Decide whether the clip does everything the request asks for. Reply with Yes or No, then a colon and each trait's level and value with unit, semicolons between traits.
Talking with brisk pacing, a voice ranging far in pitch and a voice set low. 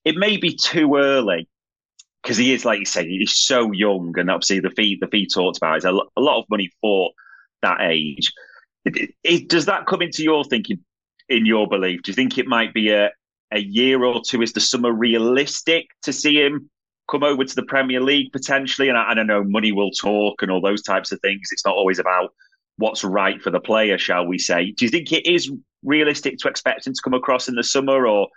Yes: fast, 235 wpm; wide, 5.7 semitones; low, 125 Hz